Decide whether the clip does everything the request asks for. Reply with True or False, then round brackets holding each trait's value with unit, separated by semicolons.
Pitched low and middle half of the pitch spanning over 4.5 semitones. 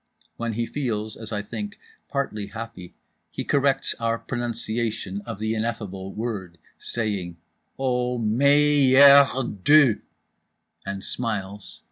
False (115 Hz; 3.9 semitones)